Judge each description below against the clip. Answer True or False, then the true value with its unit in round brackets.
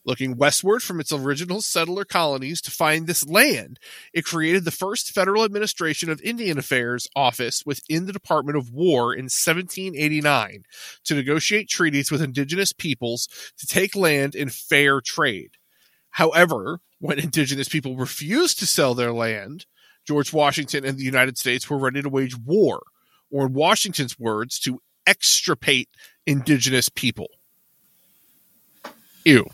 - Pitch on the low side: False (150 Hz)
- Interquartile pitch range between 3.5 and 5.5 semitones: True (4.6 semitones)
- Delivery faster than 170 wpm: False (140 wpm)